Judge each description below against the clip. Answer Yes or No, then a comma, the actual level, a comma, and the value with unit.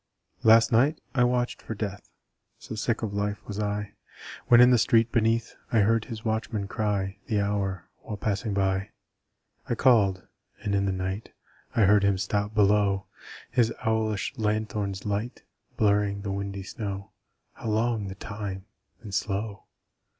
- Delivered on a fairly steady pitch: Yes, narrow, 2.1 semitones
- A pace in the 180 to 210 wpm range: No, average, 155 wpm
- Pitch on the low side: Yes, low, 105 Hz